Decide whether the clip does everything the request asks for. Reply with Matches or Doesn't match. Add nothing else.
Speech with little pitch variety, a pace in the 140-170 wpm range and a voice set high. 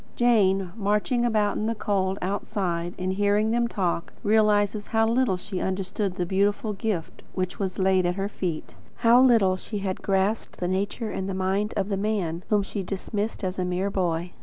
Doesn't match